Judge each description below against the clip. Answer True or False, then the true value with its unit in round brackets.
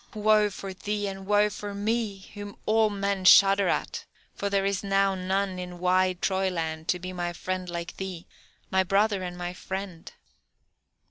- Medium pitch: False (195 Hz)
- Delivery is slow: False (165 wpm)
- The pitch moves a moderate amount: False (1.8 semitones)